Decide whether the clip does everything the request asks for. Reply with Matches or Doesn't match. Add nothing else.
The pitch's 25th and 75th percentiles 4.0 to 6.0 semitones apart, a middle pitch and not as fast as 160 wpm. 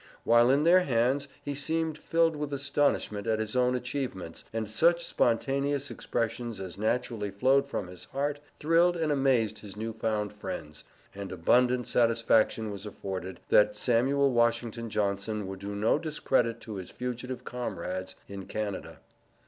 Doesn't match